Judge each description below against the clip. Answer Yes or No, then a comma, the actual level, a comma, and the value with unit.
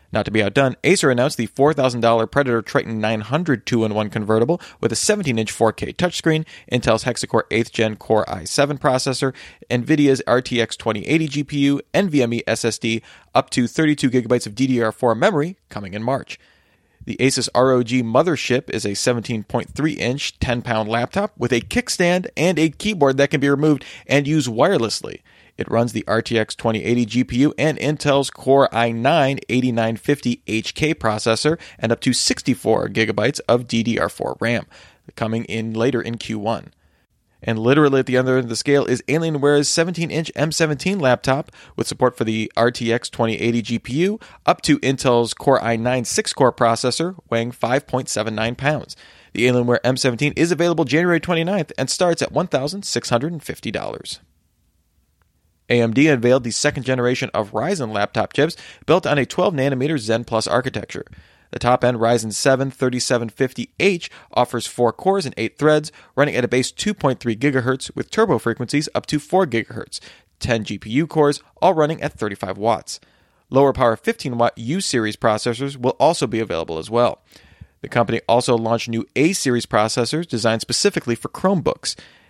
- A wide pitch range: No, average, 4.2 semitones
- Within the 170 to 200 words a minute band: No, average, 150 wpm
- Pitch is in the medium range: No, low, 125 Hz